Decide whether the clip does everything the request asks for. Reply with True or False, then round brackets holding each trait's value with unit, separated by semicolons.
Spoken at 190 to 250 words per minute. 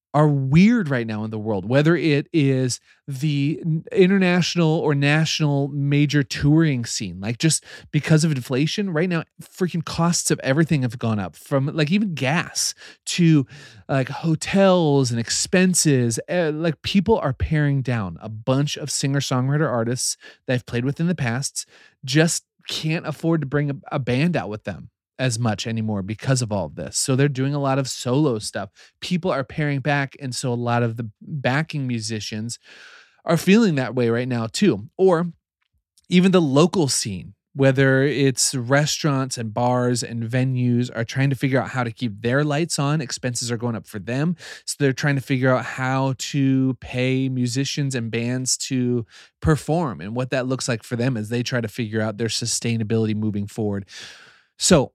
False (180 wpm)